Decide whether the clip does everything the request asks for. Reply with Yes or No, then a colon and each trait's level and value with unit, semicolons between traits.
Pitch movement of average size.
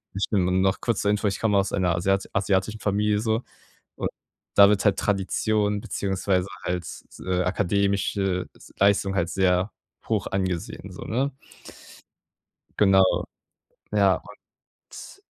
No: narrow, 1.8 semitones